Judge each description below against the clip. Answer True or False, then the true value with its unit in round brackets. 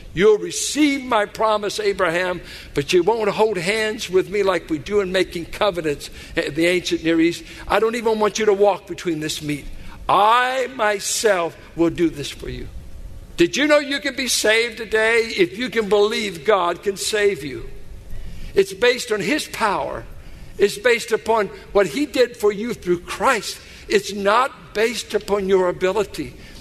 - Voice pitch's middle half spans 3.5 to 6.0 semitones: True (4.3 semitones)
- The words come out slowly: False (175 wpm)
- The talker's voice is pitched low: False (205 Hz)